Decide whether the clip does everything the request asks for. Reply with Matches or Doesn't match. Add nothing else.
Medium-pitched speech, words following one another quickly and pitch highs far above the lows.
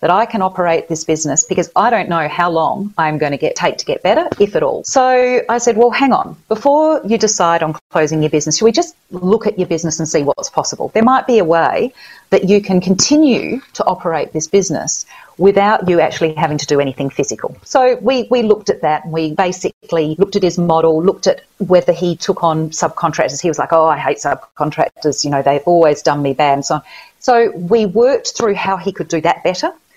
Matches